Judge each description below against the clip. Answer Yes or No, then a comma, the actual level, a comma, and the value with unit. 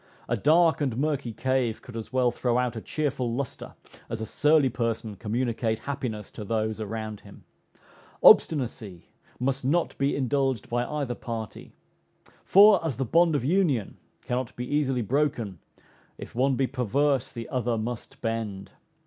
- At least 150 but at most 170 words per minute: Yes, average, 155 wpm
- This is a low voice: Yes, low, 125 Hz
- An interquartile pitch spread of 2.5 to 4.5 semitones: Yes, average, 3.6 semitones